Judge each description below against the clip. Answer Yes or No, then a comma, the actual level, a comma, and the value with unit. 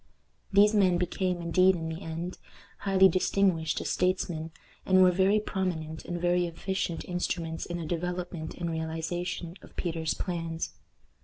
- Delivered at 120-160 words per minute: Yes, average, 145 wpm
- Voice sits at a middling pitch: Yes, medium, 175 Hz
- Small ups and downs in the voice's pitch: Yes, narrow, 2.2 semitones